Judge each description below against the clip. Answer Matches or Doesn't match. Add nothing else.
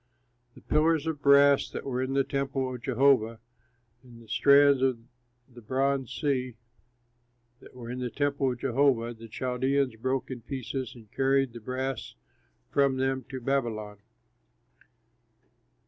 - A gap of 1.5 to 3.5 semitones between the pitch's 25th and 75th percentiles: Matches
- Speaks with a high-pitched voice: Doesn't match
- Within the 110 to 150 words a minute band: Matches